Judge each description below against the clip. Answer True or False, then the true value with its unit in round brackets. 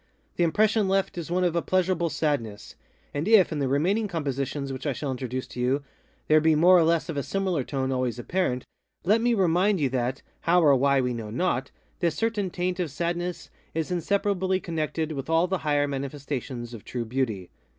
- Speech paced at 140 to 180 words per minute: False (200 wpm)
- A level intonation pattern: False (5.3 semitones)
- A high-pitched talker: False (155 Hz)